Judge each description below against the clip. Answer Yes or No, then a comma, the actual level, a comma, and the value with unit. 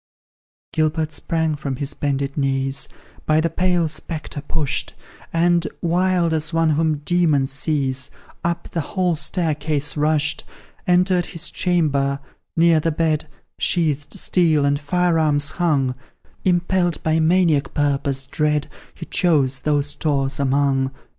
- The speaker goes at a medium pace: No, slow, 125 wpm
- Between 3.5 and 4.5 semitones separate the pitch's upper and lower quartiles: No, average, 2.9 semitones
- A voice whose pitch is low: No, medium, 155 Hz